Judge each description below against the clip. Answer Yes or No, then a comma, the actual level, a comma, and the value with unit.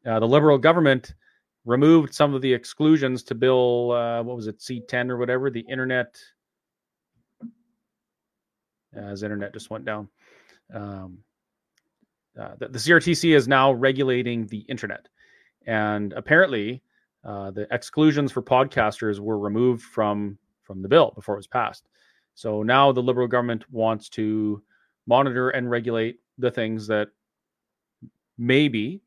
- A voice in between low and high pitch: No, low, 125 Hz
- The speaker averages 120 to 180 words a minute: Yes, average, 140 wpm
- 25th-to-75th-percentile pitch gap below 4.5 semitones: Yes, average, 3.8 semitones